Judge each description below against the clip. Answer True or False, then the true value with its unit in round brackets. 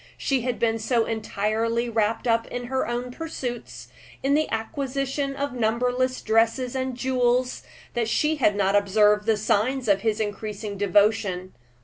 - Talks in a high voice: True (230 Hz)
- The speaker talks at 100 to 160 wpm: True (150 wpm)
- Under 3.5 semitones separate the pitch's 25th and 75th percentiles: True (3.1 semitones)